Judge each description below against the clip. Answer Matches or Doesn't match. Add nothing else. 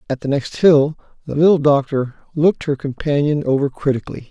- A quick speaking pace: Doesn't match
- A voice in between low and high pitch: Matches